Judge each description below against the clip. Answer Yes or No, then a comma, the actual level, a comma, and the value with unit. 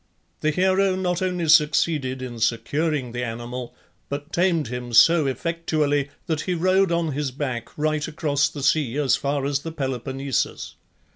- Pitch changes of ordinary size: Yes, average, 4.2 semitones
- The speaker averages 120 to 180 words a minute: Yes, average, 155 wpm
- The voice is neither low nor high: Yes, medium, 145 Hz